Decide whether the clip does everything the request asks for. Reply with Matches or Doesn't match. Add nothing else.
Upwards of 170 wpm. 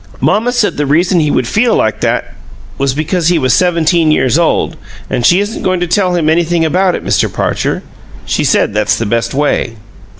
Matches